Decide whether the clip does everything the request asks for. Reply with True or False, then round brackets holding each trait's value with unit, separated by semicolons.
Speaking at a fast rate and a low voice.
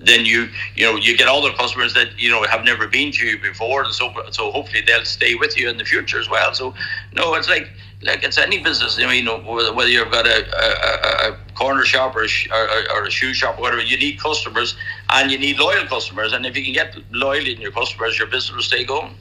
True (245 wpm; 115 Hz)